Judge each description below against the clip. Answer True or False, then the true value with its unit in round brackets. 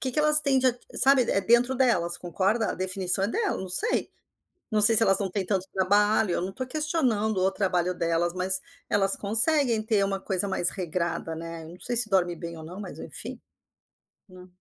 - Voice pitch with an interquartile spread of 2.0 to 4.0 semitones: False (4.5 semitones)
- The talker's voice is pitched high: True (195 Hz)